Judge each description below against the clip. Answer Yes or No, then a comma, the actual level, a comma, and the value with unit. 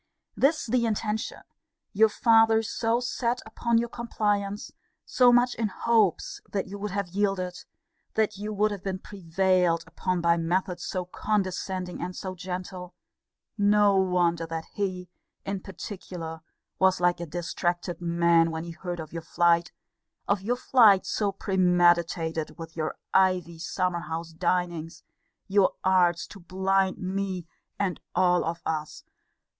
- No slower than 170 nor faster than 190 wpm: No, average, 140 wpm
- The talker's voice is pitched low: No, medium, 185 Hz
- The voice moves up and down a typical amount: Yes, average, 3.0 semitones